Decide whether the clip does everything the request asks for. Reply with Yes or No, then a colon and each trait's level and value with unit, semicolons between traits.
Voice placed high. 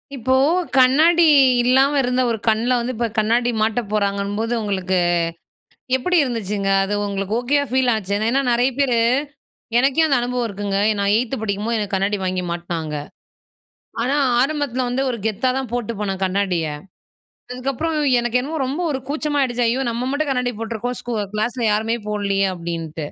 Yes: high, 235 Hz